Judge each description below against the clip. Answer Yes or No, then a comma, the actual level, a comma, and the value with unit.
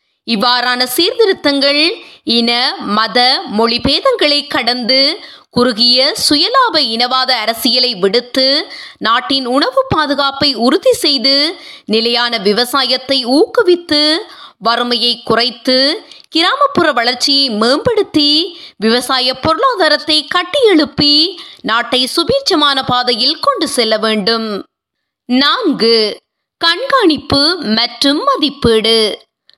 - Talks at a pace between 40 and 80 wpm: Yes, slow, 75 wpm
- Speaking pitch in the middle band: No, very high, 270 Hz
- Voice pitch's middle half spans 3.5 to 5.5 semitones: Yes, average, 4.2 semitones